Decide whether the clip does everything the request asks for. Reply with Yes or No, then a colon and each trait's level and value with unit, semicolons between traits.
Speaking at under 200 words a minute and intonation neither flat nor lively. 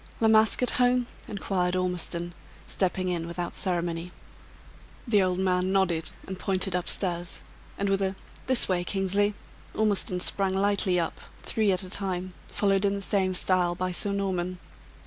No: average, 160 wpm; narrow, 1.9 semitones